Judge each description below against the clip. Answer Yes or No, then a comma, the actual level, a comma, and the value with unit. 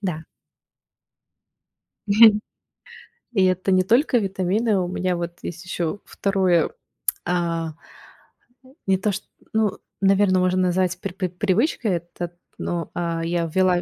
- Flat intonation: Yes, narrow, 2.3 semitones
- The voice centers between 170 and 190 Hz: Yes, medium, 185 Hz